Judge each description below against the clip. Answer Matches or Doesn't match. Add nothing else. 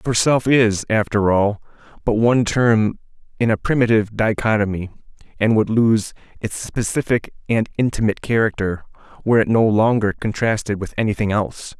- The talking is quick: Doesn't match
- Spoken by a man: Matches